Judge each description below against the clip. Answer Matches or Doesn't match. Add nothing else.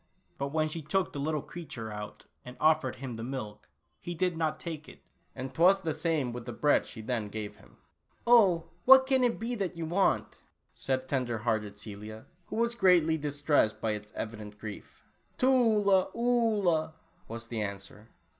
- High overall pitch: Doesn't match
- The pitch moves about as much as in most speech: Doesn't match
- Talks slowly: Doesn't match